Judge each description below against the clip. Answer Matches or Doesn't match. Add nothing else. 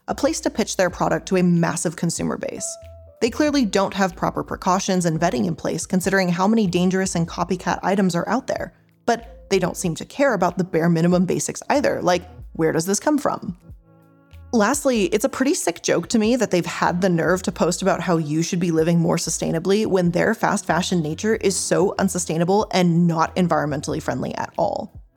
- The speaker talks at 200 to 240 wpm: Matches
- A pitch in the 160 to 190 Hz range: Matches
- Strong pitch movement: Doesn't match